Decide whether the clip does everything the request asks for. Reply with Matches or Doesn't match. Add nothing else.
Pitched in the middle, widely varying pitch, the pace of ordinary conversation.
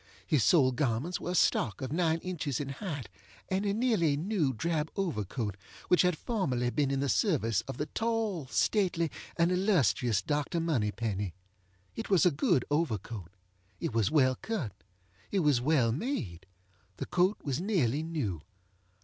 Matches